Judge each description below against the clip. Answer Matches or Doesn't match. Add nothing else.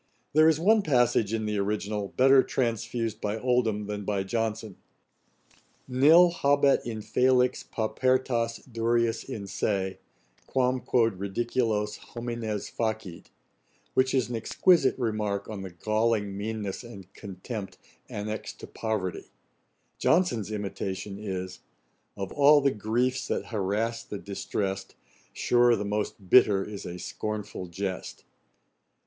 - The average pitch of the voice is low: Matches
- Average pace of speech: Doesn't match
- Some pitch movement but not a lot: Matches